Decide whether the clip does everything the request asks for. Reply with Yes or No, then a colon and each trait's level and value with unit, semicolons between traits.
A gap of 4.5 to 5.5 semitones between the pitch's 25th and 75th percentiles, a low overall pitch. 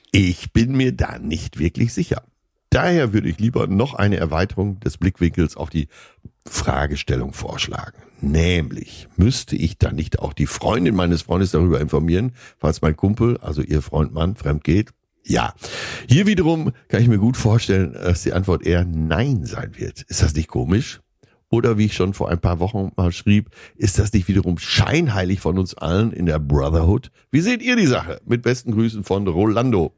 Yes: average, 5.1 semitones; very low, 95 Hz